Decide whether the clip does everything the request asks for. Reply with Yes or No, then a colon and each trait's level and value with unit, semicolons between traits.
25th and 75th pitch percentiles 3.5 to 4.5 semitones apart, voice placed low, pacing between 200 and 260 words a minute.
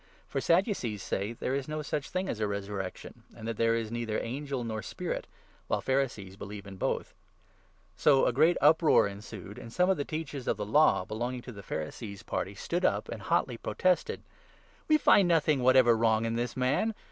No: wide, 5.6 semitones; low, 120 Hz; fast, 205 wpm